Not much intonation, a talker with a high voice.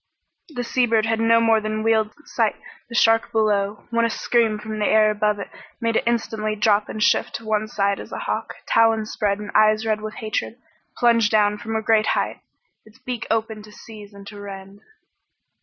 Yes: narrow, 1.2 semitones; high, 215 Hz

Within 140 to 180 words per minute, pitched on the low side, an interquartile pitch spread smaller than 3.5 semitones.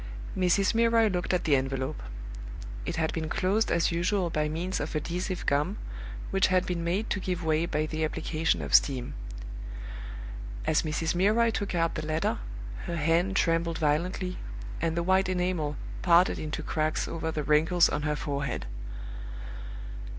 No: average, 160 wpm; medium, 170 Hz; average, 2.9 semitones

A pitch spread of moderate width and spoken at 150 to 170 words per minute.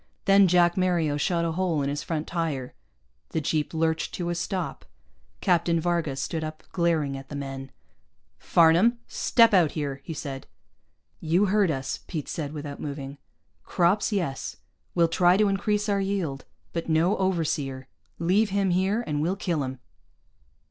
Yes: average, 4.2 semitones; average, 160 wpm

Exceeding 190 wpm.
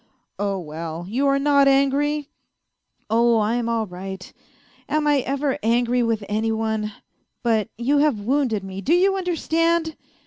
No: average, 165 wpm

